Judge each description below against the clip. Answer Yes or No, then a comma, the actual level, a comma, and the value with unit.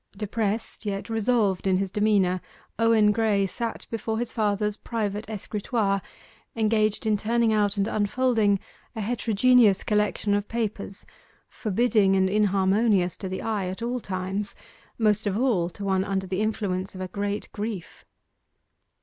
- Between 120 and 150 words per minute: Yes, average, 145 wpm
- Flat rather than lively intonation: Yes, narrow, 2.2 semitones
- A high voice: Yes, high, 210 Hz